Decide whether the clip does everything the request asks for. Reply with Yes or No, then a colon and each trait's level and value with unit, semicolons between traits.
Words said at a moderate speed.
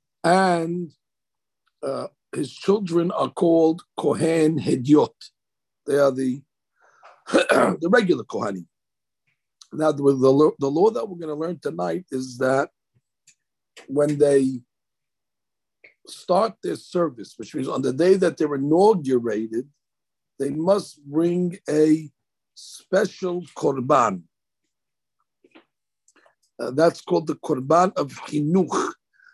No: slow, 105 wpm